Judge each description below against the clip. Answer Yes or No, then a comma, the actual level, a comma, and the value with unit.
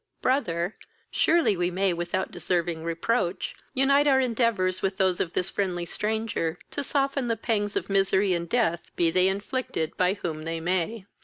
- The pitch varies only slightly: No, average, 4.9 semitones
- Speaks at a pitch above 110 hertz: Yes, high, 190 Hz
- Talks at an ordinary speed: Yes, average, 165 wpm